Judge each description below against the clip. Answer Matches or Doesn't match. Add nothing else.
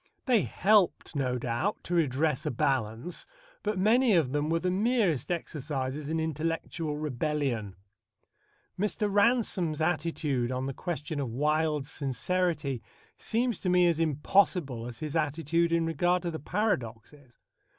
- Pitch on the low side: Doesn't match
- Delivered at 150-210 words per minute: Doesn't match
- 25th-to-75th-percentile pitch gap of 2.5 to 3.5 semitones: Doesn't match